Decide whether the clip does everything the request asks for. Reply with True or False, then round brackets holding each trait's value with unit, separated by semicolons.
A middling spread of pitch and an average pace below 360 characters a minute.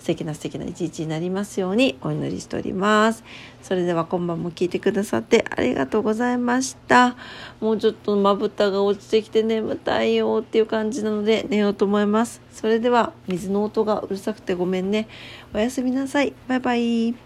False (3.0 semitones; 405 characters per minute)